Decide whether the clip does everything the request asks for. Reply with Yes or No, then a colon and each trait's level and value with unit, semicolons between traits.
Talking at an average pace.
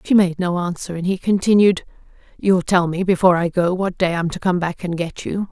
No: fast, 240 wpm